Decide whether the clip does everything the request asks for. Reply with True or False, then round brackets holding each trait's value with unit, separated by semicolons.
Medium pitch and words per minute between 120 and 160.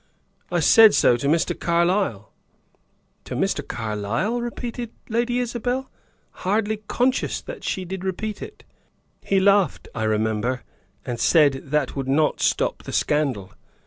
True (175 Hz; 135 wpm)